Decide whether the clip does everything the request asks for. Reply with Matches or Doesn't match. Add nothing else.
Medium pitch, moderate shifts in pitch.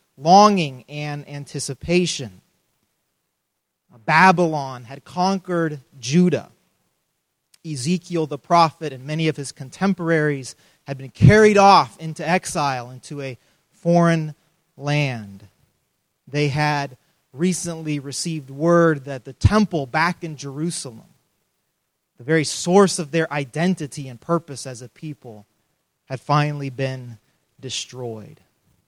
Matches